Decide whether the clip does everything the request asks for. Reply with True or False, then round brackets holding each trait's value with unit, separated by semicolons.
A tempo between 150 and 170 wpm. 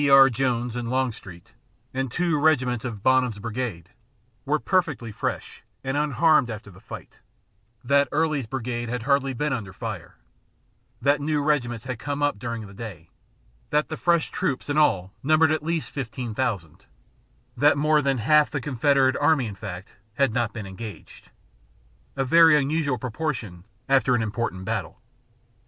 True (155 wpm)